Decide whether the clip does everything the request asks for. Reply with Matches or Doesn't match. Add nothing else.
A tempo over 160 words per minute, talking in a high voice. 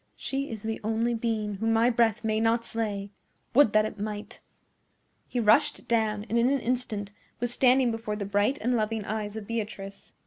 Matches